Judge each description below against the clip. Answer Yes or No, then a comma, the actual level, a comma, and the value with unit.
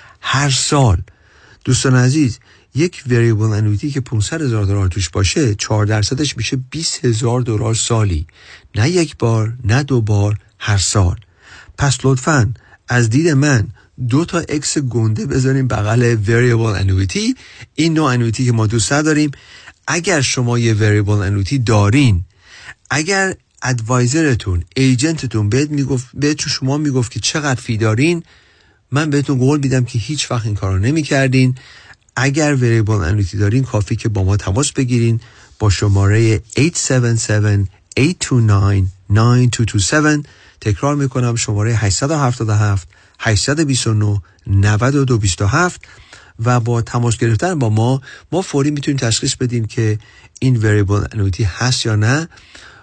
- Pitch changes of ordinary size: Yes, average, 4.6 semitones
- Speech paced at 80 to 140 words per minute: Yes, average, 130 wpm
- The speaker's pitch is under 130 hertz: Yes, low, 120 Hz